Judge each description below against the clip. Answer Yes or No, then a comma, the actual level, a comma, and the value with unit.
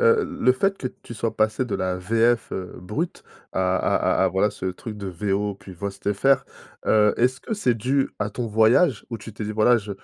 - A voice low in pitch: Yes, low, 110 Hz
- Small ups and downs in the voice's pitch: No, average, 3.9 semitones